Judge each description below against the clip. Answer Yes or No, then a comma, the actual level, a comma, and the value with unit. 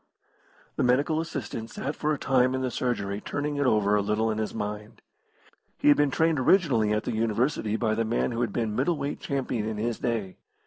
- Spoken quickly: Yes, fast, 215 wpm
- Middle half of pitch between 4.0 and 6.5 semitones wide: Yes, average, 4.5 semitones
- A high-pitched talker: No, low, 120 Hz